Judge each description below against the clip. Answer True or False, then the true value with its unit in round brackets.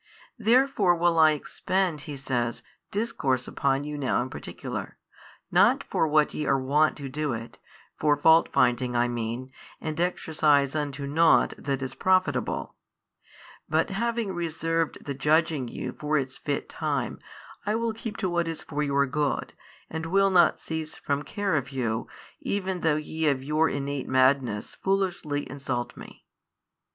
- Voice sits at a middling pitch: True (150 Hz)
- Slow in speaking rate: False (155 wpm)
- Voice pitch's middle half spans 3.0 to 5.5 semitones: True (3.9 semitones)